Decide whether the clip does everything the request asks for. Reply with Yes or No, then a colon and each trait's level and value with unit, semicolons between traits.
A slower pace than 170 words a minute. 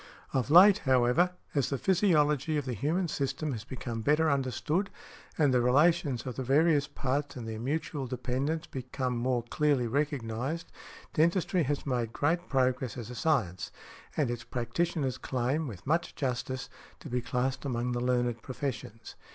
Yes: average, 160 wpm